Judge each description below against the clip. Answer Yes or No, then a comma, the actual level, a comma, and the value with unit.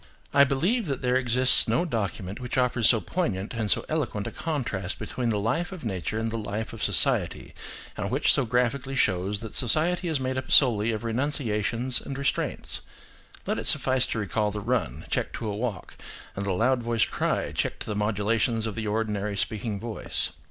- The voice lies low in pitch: Yes, low, 115 Hz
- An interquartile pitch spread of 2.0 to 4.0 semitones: Yes, average, 3.7 semitones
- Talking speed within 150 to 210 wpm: Yes, average, 195 wpm